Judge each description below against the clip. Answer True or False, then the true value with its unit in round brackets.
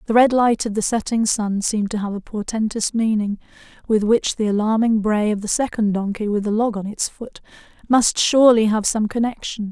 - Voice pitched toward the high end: True (215 Hz)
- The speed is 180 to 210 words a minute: True (205 wpm)